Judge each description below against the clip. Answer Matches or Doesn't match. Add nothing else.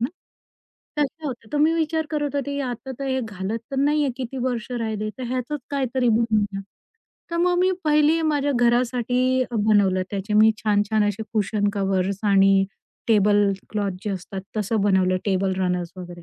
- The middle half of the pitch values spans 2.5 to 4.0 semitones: Doesn't match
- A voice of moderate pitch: Doesn't match